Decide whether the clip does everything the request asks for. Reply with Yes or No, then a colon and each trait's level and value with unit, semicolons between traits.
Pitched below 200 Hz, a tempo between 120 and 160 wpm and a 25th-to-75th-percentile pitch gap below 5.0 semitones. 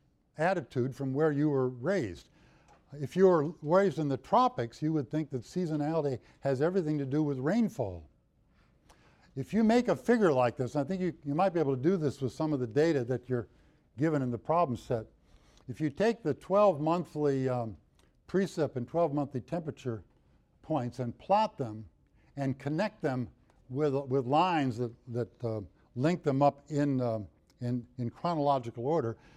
No: medium, 140 Hz; average, 180 wpm; average, 4.4 semitones